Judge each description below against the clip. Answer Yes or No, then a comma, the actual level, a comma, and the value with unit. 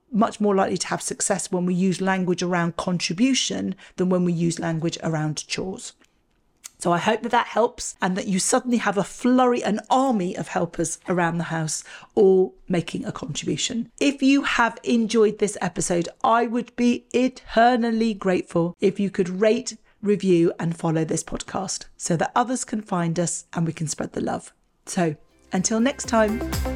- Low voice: No, high, 190 Hz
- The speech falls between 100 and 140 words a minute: No, average, 175 wpm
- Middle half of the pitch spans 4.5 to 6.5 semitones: Yes, average, 5.0 semitones